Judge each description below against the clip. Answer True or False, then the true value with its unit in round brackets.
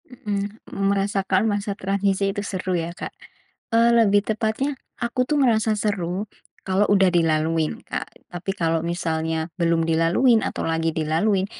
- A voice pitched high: True (195 Hz)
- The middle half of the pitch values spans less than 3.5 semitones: False (4.2 semitones)